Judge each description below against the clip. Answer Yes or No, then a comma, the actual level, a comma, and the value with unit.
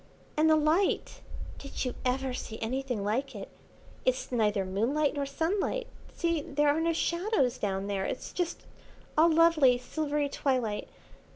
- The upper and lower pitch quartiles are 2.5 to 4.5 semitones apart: No, average, 4.9 semitones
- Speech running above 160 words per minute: No, average, 150 wpm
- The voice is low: No, very high, 280 Hz